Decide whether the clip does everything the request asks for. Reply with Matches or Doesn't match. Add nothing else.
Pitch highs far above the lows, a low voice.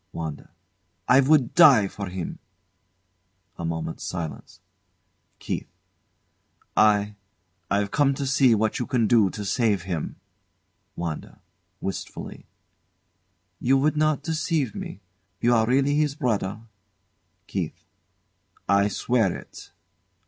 Matches